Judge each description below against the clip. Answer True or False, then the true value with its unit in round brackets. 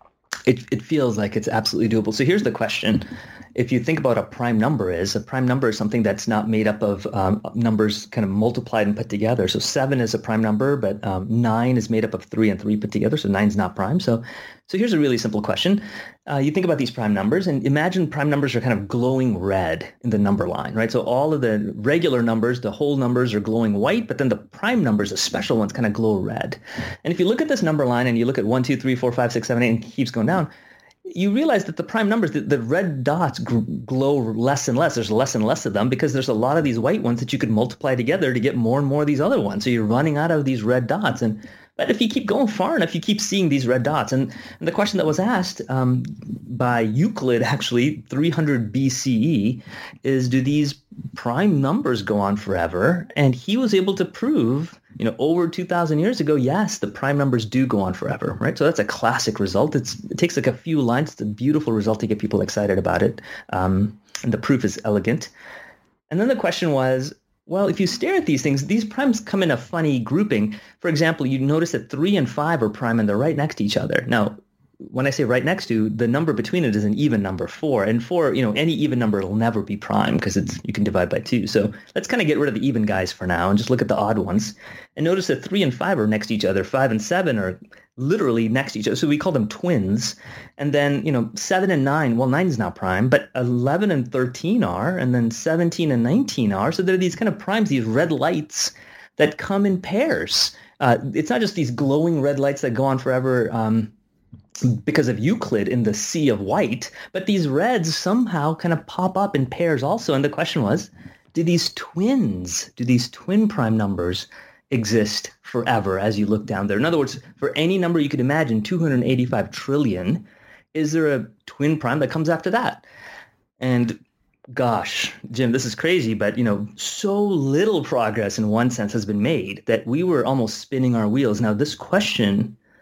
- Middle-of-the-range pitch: False (130 Hz)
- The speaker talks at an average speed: False (235 wpm)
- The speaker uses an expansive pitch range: True (6.4 semitones)